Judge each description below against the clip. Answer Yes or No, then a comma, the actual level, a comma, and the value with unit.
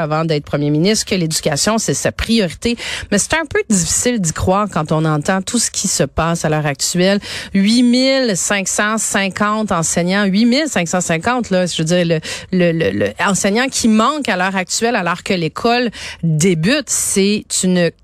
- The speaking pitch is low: No, high, 195 Hz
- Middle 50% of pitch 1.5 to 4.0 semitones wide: No, average, 4.8 semitones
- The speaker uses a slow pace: No, average, 175 wpm